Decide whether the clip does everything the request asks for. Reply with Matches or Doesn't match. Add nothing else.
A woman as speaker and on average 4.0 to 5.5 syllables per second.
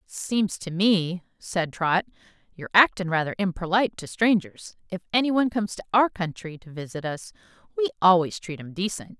Matches